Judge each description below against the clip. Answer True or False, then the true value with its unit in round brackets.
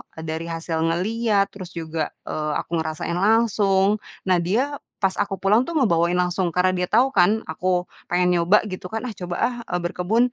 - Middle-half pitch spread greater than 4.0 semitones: False (3.6 semitones)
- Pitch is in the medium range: True (180 Hz)